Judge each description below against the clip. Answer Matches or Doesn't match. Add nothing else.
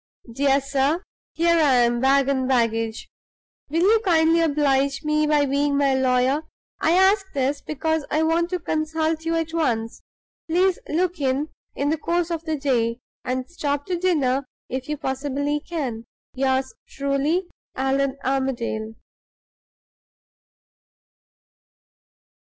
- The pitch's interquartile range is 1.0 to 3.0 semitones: Doesn't match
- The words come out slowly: Matches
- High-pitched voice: Matches